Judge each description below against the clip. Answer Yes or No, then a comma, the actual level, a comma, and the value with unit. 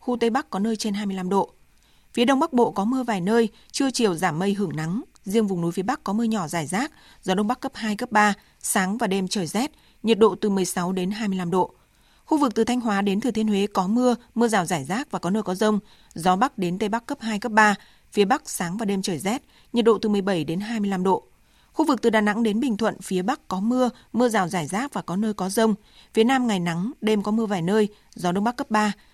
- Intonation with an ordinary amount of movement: Yes, average, 3.4 semitones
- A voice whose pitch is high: Yes, high, 215 Hz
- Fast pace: Yes, fast, 265 wpm